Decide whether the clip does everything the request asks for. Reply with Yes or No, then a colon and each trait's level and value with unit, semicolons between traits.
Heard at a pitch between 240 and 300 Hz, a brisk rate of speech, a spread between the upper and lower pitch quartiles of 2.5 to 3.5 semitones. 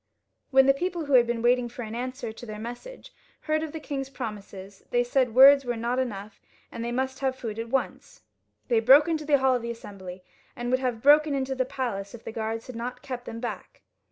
Yes: high, 245 Hz; fast, 225 wpm; average, 2.9 semitones